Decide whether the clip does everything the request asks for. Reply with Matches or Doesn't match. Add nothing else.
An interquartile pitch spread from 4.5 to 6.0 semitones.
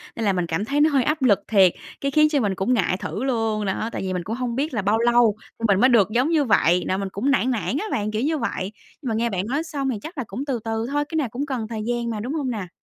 Matches